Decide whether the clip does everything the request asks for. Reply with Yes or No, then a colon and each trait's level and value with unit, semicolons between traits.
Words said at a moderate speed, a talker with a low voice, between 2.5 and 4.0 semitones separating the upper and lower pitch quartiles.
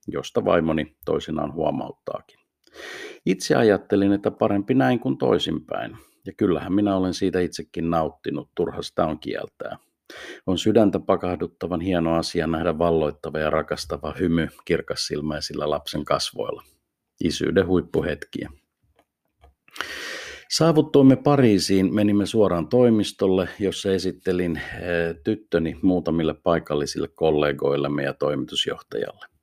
No: average, 105 wpm; very low, 95 Hz; average, 4.7 semitones